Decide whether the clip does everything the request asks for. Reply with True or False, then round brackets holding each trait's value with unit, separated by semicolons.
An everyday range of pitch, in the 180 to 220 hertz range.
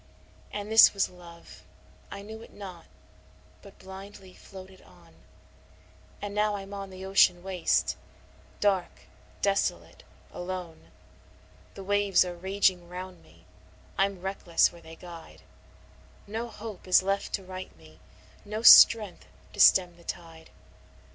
False (2.2 semitones; 190 Hz)